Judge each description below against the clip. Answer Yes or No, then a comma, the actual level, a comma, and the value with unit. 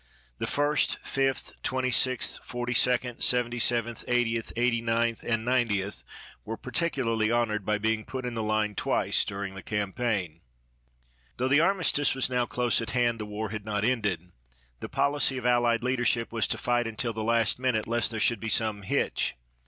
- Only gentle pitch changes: Yes, narrow, 2.3 semitones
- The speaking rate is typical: Yes, average, 175 wpm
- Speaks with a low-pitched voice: Yes, low, 115 Hz